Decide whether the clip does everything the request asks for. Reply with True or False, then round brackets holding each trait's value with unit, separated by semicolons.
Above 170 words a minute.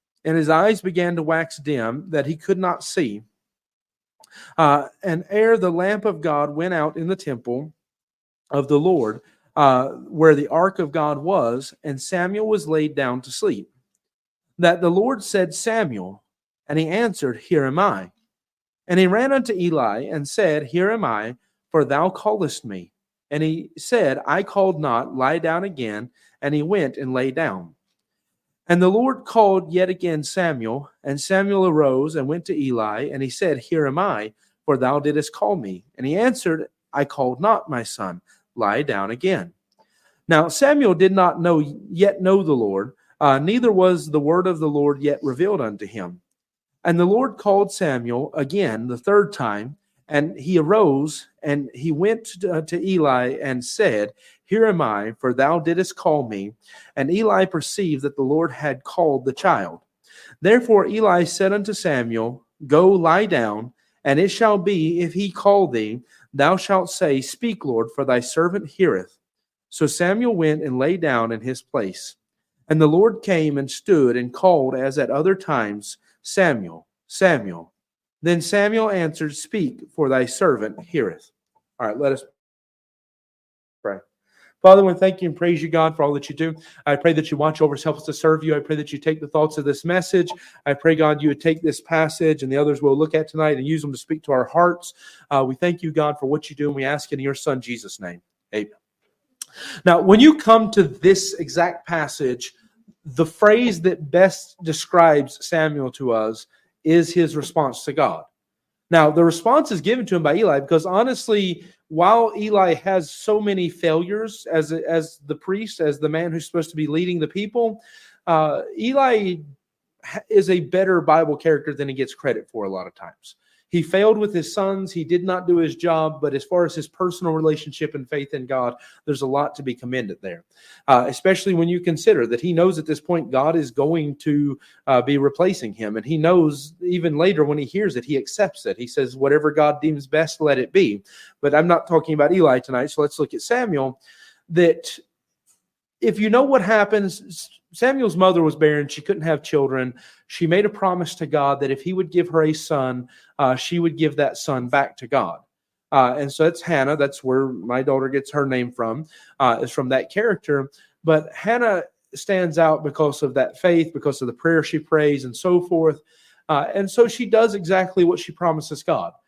True (195 wpm)